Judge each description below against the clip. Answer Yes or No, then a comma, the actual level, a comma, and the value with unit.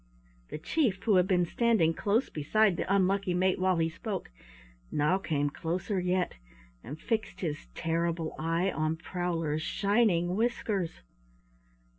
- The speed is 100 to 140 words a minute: Yes, slow, 135 wpm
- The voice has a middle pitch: Yes, medium, 180 Hz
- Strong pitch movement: No, average, 3.4 semitones